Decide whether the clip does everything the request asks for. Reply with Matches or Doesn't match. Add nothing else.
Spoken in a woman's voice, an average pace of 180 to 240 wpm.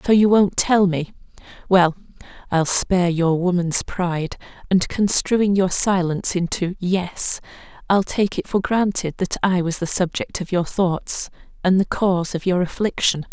Doesn't match